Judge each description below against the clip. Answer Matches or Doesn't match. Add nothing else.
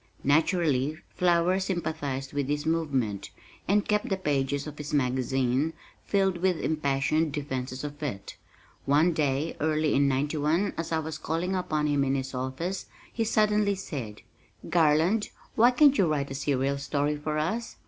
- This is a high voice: Doesn't match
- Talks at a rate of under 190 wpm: Matches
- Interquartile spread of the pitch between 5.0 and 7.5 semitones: Doesn't match